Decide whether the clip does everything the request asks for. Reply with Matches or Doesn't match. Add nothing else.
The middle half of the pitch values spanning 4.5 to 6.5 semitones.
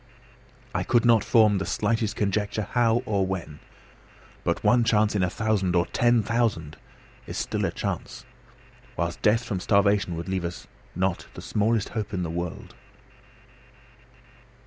Doesn't match